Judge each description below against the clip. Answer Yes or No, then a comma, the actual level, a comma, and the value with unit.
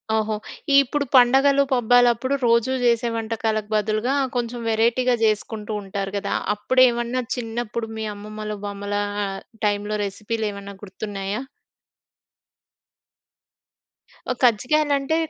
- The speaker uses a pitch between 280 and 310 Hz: No, high, 225 Hz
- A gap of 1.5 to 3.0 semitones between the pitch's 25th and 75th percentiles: Yes, average, 2.7 semitones